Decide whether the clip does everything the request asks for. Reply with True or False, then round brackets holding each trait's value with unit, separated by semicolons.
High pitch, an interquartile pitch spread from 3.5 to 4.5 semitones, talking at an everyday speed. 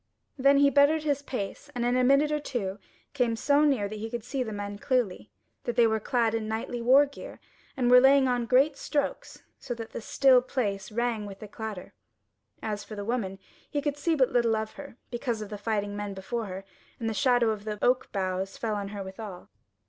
False (235 Hz; 4.0 semitones; 220 wpm)